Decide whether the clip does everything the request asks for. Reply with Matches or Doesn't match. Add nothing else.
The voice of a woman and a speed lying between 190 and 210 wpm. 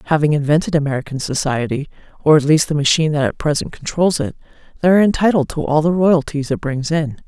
Matches